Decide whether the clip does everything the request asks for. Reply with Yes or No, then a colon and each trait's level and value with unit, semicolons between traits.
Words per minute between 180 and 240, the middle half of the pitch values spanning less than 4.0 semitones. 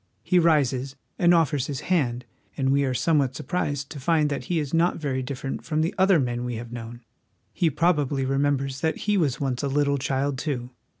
Yes: average, 200 wpm; average, 3.5 semitones